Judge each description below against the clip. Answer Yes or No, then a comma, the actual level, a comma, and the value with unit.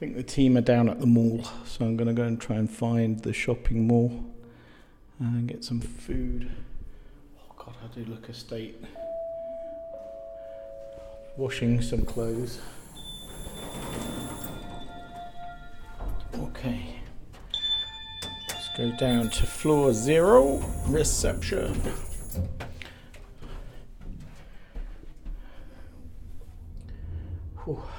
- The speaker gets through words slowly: Yes, slow, 90 wpm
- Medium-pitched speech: No, low, 115 Hz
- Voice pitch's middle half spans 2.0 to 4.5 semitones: No, average, 5.1 semitones